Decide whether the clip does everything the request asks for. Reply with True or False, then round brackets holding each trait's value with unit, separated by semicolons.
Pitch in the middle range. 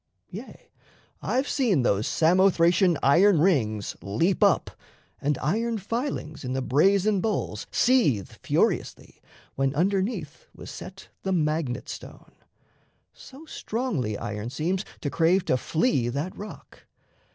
True (170 Hz)